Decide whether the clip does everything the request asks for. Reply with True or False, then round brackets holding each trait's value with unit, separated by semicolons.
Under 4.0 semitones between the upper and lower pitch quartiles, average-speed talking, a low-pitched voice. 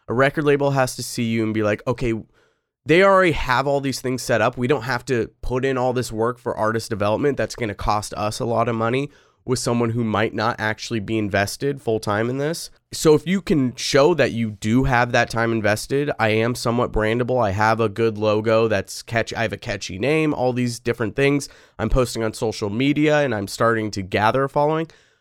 False (3.5 semitones; 225 wpm; 120 Hz)